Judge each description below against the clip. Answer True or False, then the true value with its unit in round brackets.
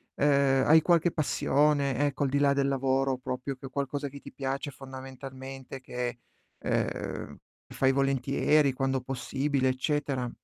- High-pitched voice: False (135 Hz)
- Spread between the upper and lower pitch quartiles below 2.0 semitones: True (1.3 semitones)